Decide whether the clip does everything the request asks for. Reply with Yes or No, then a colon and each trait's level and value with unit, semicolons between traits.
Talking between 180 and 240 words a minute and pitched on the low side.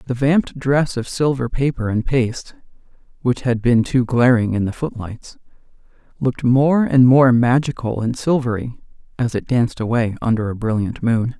No: average, 165 wpm; low, 125 Hz